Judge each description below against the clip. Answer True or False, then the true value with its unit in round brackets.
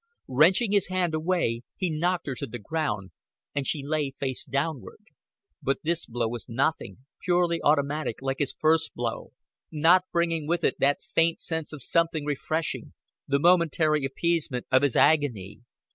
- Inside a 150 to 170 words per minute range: True (160 wpm)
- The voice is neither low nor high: True (155 Hz)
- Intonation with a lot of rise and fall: False (3.8 semitones)